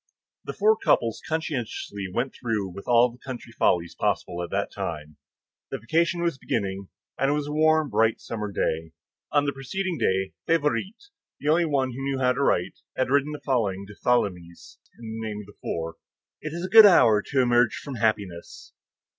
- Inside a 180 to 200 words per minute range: Yes, average, 190 wpm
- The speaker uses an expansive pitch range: Yes, wide, 6.8 semitones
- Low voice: Yes, low, 120 Hz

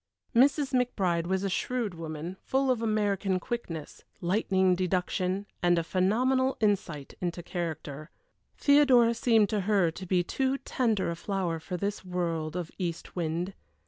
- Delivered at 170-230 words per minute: No, average, 145 wpm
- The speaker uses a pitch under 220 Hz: Yes, high, 190 Hz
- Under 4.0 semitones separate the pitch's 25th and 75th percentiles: No, average, 4.7 semitones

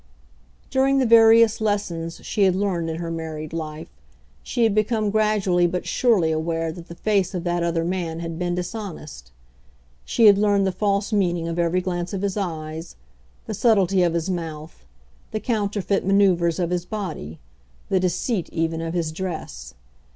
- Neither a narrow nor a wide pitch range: Yes, average, 3.7 semitones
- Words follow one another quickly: No, average, 170 wpm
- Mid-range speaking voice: Yes, medium, 180 Hz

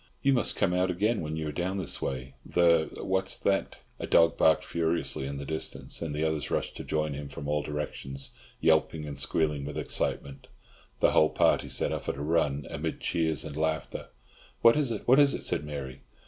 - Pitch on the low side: Yes, very low, 80 Hz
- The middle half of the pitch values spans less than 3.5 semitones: Yes, average, 3.1 semitones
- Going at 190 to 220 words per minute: Yes, fast, 205 wpm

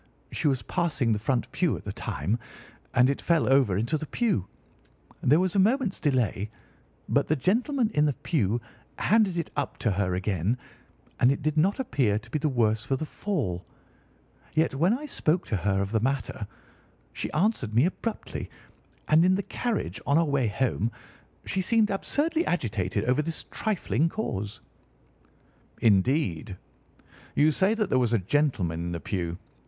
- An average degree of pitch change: No, wide, 8.8 semitones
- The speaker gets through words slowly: No, average, 170 wpm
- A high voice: No, medium, 140 Hz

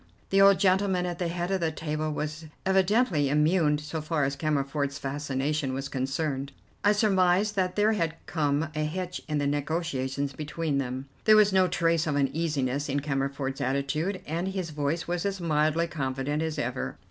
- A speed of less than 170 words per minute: No, average, 175 wpm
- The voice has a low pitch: No, medium, 155 Hz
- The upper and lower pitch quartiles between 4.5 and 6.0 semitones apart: No, average, 4.0 semitones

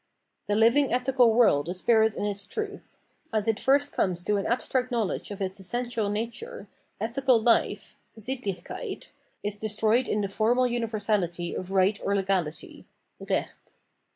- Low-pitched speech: No, high, 220 Hz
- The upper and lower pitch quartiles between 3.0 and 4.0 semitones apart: Yes, average, 3.5 semitones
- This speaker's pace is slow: No, average, 150 wpm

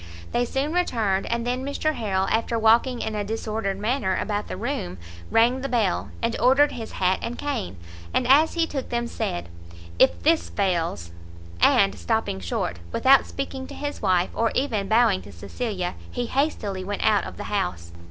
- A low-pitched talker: No, high, 225 Hz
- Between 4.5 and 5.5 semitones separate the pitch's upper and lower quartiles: Yes, average, 5.2 semitones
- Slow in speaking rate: No, average, 180 wpm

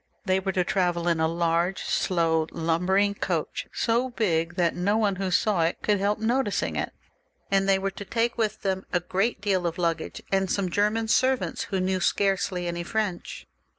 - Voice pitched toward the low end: No, high, 190 Hz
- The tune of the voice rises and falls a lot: No, average, 3.0 semitones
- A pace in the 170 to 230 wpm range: Yes, average, 185 wpm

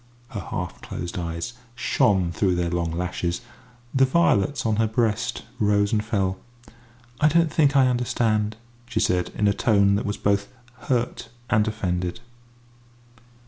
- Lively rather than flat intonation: No, average, 4.5 semitones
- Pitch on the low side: Yes, low, 105 Hz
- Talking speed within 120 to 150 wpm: Yes, average, 145 wpm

